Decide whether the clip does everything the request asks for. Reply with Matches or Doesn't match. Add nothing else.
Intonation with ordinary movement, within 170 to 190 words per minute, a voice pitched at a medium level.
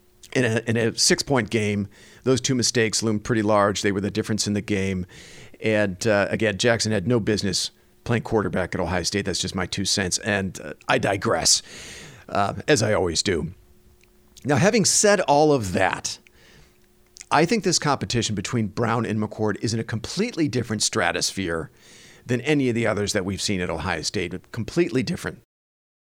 Doesn't match